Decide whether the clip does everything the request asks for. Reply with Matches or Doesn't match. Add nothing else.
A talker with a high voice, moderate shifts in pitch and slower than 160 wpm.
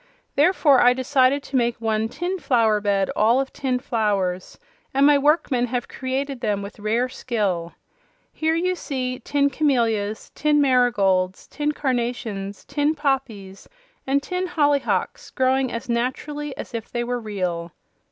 Matches